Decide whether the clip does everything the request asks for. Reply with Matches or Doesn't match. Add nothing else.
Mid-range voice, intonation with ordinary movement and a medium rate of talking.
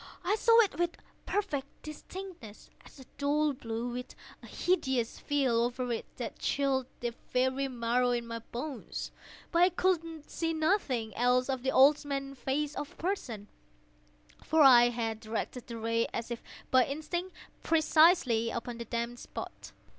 Doesn't match